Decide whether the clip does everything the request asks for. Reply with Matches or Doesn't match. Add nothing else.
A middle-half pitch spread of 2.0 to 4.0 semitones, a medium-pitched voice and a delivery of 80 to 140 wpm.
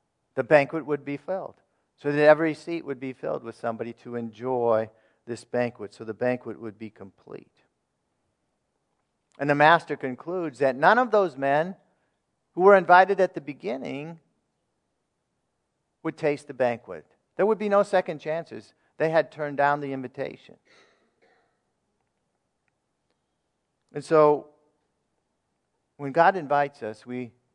Doesn't match